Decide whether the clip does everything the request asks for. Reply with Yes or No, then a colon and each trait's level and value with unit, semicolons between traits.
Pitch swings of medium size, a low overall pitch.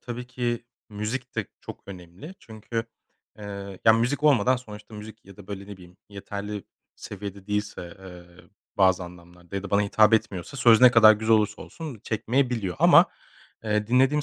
Yes: average, 3.1 semitones; low, 105 Hz